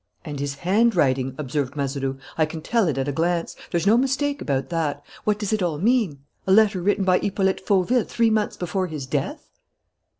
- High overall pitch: No, medium, 175 Hz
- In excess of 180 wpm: Yes, average, 195 wpm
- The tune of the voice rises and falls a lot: Yes, wide, 6.6 semitones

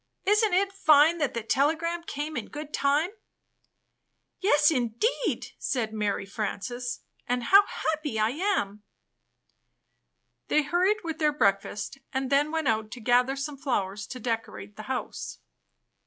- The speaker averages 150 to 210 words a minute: No, average, 140 wpm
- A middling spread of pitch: No, wide, 6.0 semitones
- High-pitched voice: Yes, very high, 280 Hz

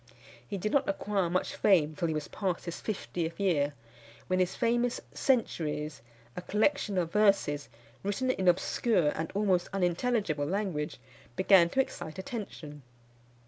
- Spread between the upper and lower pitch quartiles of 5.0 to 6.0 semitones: No, average, 4.4 semitones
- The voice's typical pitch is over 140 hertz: Yes, medium, 185 Hz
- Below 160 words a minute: Yes, average, 140 wpm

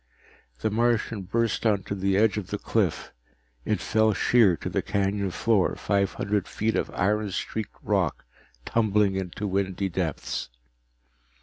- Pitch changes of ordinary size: No, narrow, 2.2 semitones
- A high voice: No, low, 100 Hz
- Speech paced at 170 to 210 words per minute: No, average, 140 wpm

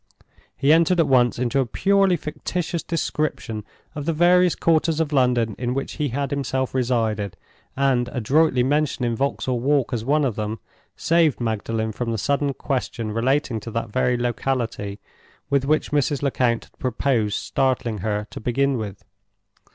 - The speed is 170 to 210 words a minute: No, average, 160 wpm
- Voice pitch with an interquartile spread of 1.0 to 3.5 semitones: No, average, 4.0 semitones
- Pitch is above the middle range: No, low, 130 Hz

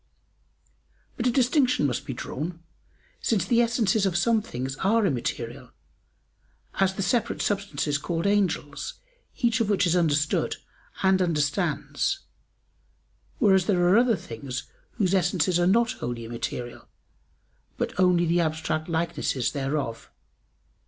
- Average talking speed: No, slow, 125 wpm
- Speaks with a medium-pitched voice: Yes, medium, 175 Hz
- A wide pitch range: Yes, wide, 6.0 semitones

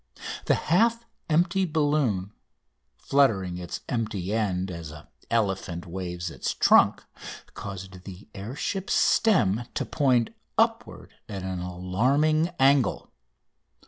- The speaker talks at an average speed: No, slow, 110 wpm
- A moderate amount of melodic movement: No, wide, 7.7 semitones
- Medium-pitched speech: No, low, 105 Hz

